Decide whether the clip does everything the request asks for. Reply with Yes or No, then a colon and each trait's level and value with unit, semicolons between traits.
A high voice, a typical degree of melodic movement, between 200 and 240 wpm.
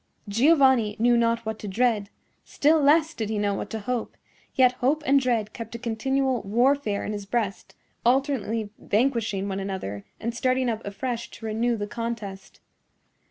No: high, 230 Hz; average, 3.6 semitones; average, 165 wpm